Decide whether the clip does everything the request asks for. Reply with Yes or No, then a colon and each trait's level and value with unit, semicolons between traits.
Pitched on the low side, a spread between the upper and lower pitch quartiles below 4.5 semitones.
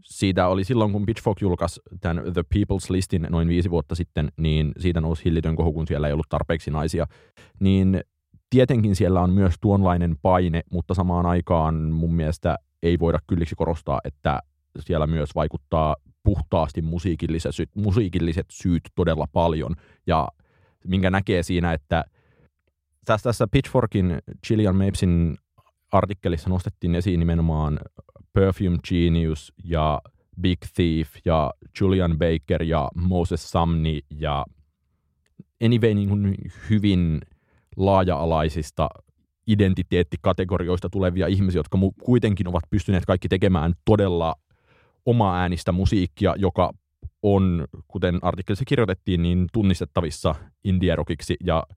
Yes: very low, 90 Hz; average, 2.8 semitones